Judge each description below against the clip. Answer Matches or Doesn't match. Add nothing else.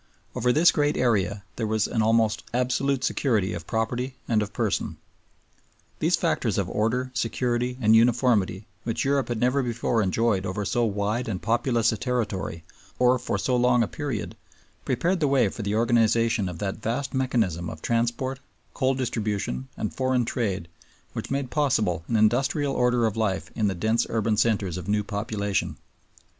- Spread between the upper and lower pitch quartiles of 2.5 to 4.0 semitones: Matches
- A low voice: Matches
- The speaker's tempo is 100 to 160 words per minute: Doesn't match